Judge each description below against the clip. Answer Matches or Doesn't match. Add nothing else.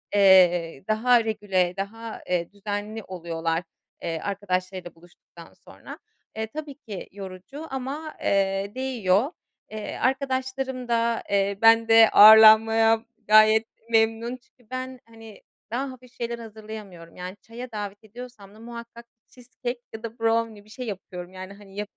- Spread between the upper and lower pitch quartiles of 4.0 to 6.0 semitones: Doesn't match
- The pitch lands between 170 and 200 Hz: Doesn't match